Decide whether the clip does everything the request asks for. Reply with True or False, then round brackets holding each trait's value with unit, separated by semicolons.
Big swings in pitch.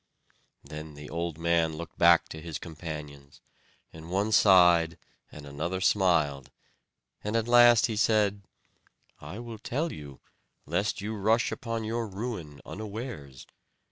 True (5.9 semitones)